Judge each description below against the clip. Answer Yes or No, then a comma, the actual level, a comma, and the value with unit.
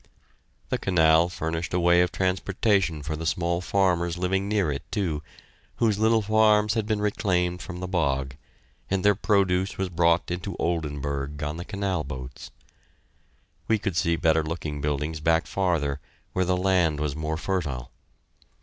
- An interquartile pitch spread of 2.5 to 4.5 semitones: Yes, average, 3.6 semitones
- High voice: No, very low, 85 Hz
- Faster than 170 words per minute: No, average, 160 wpm